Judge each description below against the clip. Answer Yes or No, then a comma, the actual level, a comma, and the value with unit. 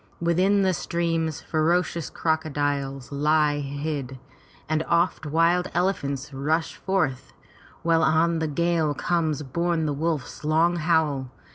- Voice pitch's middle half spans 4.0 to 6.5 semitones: No, narrow, 2.6 semitones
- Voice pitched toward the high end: No, medium, 160 Hz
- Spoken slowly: Yes, slow, 120 wpm